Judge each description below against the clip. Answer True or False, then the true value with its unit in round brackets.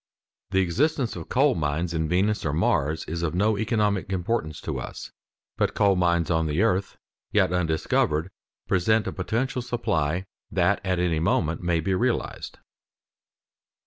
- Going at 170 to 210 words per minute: False (150 wpm)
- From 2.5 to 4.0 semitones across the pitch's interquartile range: False (4.6 semitones)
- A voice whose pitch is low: True (90 Hz)